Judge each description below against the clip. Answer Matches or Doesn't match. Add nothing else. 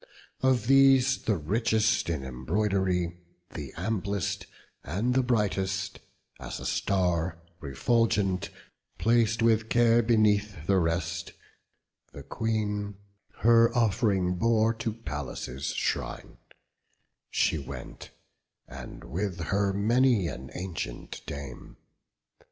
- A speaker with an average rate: Doesn't match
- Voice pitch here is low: Matches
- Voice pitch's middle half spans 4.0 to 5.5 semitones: Matches